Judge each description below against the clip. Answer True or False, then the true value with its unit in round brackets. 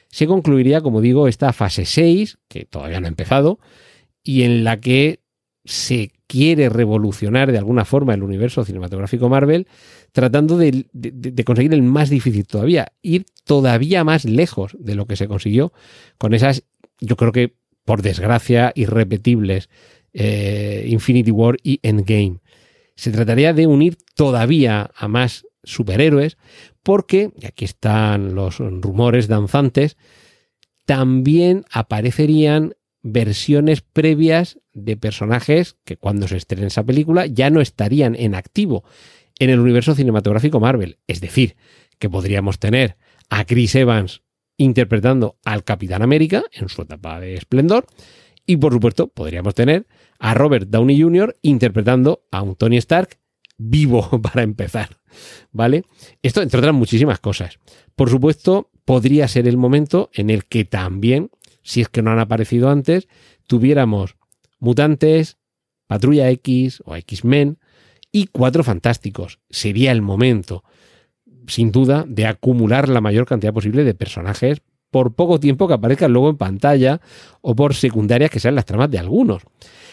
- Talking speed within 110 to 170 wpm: True (145 wpm)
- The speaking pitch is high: False (125 Hz)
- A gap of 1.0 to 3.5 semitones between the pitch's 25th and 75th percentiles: False (4.8 semitones)